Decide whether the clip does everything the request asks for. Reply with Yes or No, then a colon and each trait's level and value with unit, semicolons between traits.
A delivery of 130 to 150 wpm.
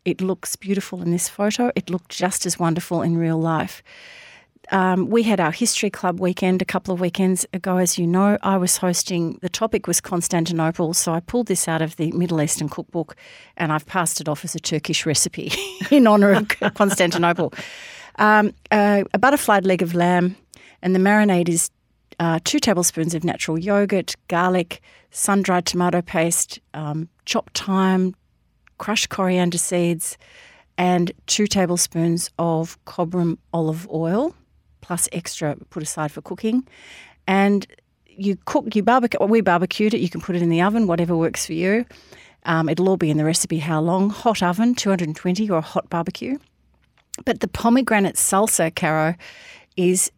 No: average, 170 wpm